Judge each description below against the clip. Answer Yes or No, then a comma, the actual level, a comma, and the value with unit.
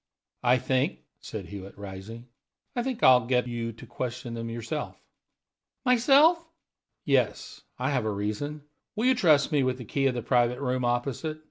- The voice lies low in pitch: Yes, low, 125 Hz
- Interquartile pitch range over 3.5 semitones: Yes, average, 4.4 semitones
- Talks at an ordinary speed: Yes, average, 165 wpm